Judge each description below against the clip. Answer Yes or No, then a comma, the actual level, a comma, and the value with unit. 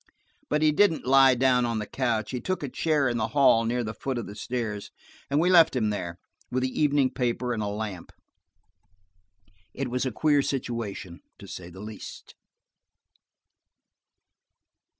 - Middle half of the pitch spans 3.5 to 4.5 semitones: Yes, average, 4.1 semitones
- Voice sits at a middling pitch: No, low, 125 Hz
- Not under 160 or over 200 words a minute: Yes, average, 170 wpm